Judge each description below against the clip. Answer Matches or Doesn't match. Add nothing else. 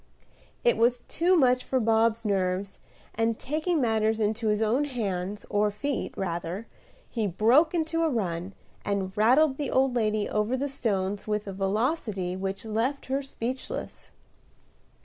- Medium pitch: Doesn't match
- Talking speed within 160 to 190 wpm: Doesn't match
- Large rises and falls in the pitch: Doesn't match